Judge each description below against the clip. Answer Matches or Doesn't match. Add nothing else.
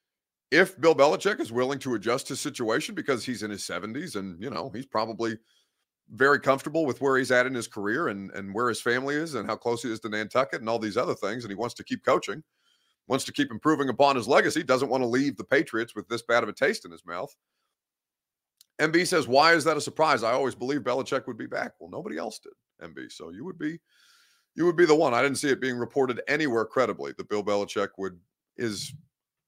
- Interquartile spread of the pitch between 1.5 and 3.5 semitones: Doesn't match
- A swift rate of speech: Matches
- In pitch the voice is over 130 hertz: Doesn't match